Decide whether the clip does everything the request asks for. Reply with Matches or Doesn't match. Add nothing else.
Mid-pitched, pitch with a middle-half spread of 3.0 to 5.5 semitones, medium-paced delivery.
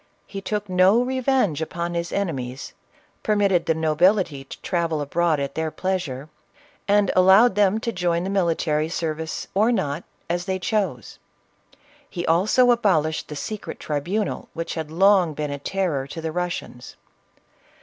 Matches